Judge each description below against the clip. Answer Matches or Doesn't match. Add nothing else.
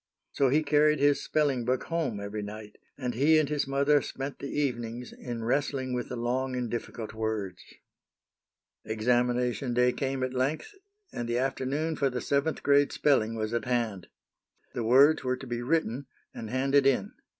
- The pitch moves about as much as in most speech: Matches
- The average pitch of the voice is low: Matches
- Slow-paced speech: Doesn't match